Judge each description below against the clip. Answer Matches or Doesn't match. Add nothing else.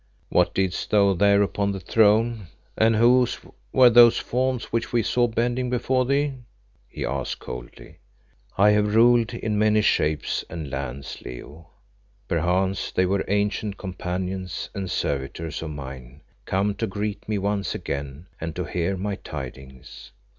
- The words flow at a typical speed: Matches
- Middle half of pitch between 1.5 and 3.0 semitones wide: Doesn't match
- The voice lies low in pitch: Matches